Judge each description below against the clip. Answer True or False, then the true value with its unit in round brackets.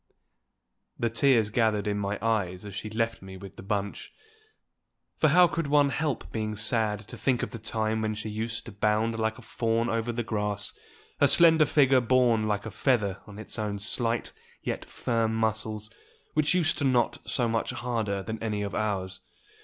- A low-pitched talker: True (110 Hz)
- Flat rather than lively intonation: True (2.2 semitones)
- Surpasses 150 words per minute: True (185 wpm)